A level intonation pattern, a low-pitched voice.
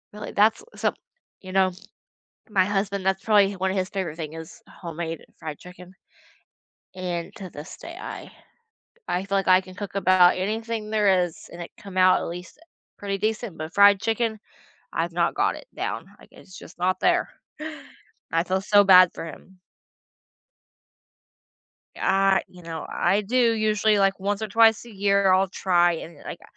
No: narrow, 2.3 semitones; high, 190 Hz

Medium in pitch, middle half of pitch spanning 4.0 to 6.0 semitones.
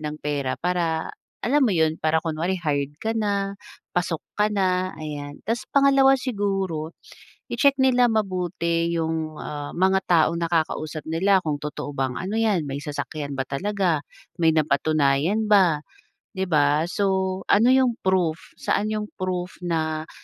Yes: medium, 170 Hz; average, 4.4 semitones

